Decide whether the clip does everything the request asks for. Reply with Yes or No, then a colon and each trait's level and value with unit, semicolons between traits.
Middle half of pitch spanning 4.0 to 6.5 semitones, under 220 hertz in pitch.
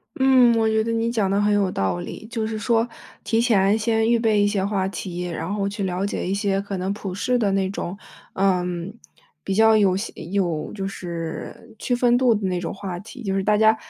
No: average, 2.8 semitones; high, 200 Hz